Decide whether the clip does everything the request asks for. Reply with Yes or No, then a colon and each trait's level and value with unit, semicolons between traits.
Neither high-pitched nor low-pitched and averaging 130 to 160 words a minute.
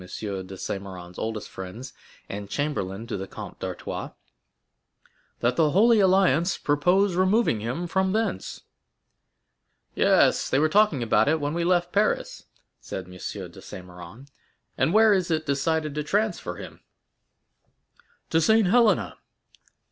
Yes: medium, 150 Hz; average, 140 wpm